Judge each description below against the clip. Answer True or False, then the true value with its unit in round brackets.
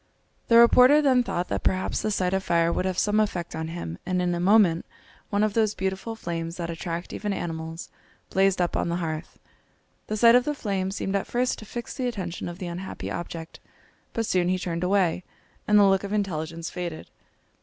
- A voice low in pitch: False (185 Hz)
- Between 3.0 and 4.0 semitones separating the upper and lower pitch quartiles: True (3.6 semitones)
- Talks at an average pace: False (210 wpm)